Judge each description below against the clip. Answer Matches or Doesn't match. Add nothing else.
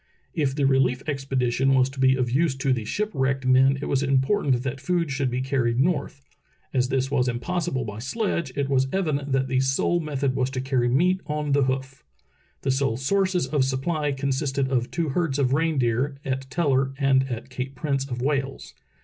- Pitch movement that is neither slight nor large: Doesn't match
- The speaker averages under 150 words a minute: Doesn't match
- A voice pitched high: Doesn't match